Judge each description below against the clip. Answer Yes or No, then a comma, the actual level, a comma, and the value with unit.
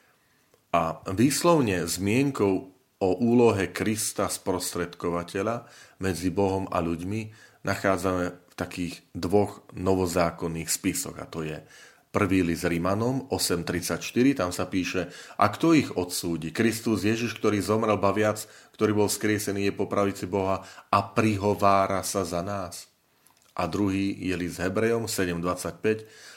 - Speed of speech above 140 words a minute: No, average, 125 wpm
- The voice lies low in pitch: Yes, very low, 95 Hz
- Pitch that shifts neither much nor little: Yes, average, 3.0 semitones